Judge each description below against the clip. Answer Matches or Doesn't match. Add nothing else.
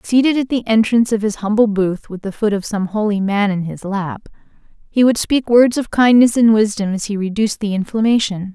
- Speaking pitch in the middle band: Doesn't match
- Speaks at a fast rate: Matches